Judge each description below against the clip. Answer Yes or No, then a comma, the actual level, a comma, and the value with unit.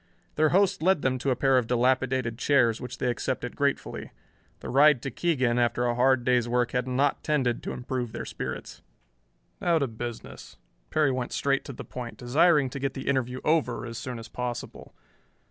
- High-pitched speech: No, low, 130 Hz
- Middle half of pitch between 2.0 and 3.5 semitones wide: Yes, narrow, 2.4 semitones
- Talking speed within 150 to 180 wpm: No, average, 190 wpm